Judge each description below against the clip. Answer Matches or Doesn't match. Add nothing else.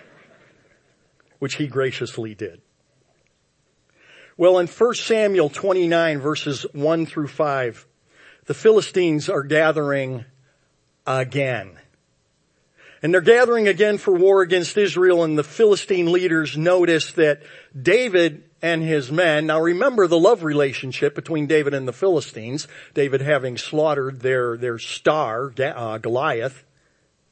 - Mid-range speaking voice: Matches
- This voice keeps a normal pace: Doesn't match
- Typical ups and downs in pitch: Matches